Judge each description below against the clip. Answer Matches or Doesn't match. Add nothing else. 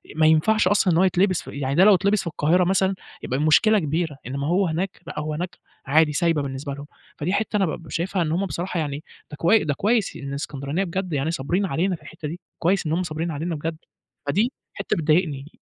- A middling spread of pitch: Matches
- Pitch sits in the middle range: Matches